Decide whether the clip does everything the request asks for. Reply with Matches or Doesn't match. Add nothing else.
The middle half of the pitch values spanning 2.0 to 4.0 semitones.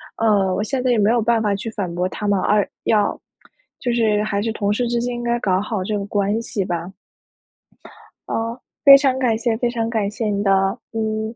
Matches